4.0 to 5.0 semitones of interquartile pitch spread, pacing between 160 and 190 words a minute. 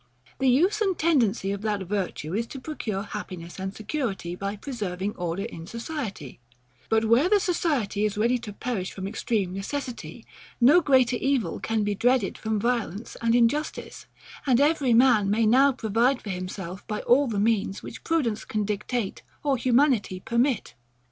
Yes: average, 4.7 semitones; average, 165 wpm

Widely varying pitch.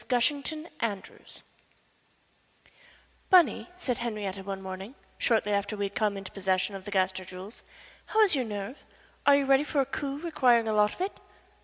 Yes: wide, 5.9 semitones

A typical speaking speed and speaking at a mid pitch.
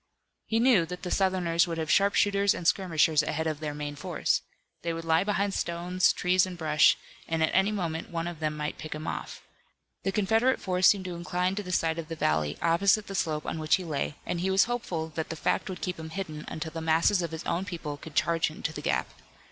No: fast, 235 wpm; medium, 170 Hz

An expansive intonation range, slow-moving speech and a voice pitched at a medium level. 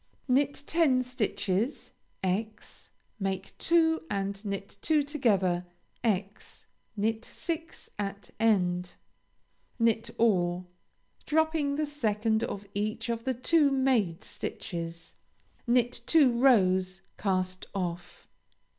No: wide, 5.8 semitones; slow, 100 wpm; high, 220 Hz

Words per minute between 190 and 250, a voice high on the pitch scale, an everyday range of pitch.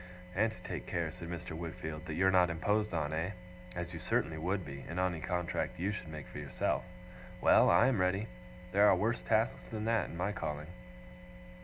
No: average, 200 wpm; very low, 90 Hz; average, 4.0 semitones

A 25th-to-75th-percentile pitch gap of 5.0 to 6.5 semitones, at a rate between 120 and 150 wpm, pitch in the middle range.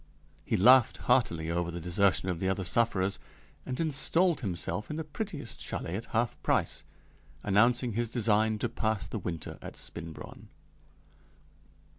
No: average, 5.3 semitones; average, 145 wpm; low, 105 Hz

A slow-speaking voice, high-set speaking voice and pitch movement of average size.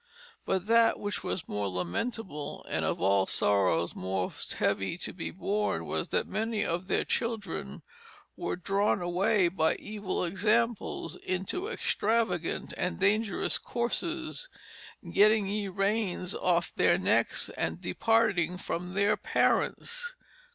Yes: slow, 125 wpm; high, 195 Hz; average, 4.4 semitones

